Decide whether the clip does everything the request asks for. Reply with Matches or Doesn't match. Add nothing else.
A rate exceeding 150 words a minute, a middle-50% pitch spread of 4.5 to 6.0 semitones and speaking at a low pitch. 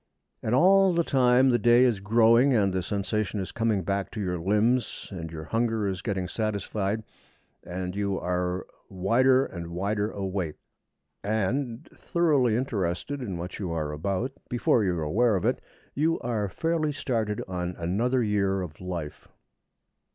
Matches